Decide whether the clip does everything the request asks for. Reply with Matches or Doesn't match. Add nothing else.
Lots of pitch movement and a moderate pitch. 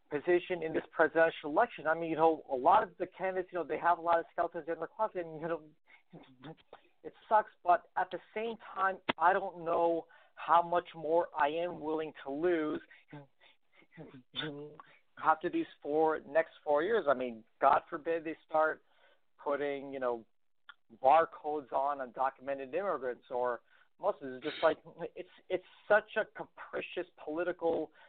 Doesn't match